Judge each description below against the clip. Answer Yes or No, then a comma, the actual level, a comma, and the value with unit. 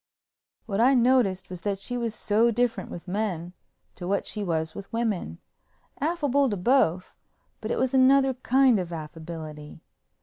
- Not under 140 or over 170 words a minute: Yes, average, 155 wpm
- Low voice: No, high, 210 Hz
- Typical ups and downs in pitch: No, wide, 6.1 semitones